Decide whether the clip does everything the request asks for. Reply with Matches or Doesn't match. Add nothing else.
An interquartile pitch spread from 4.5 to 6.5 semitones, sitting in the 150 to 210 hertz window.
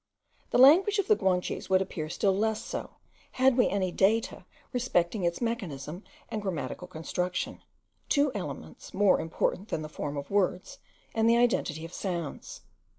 Matches